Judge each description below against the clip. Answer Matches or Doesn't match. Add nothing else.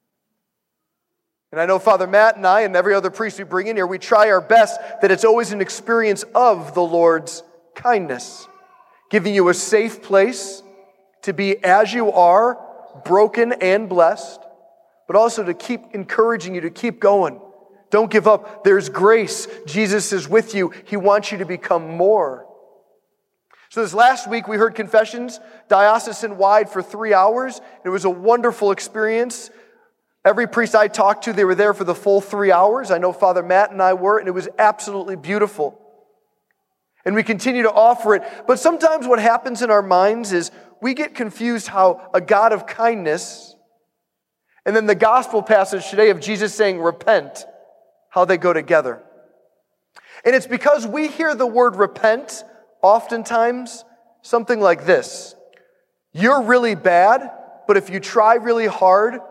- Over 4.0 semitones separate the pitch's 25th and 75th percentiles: Doesn't match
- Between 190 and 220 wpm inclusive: Doesn't match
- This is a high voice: Matches